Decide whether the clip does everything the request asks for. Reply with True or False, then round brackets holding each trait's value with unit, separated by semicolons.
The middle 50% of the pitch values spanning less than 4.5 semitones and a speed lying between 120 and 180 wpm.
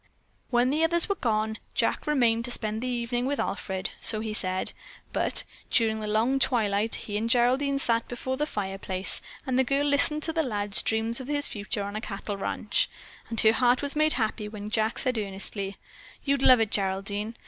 False (3.9 semitones; 195 wpm)